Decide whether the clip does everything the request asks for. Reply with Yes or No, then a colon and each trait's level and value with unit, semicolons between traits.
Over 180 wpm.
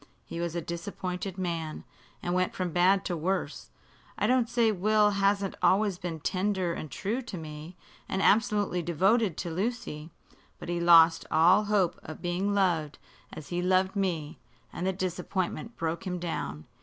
No: average, 165 wpm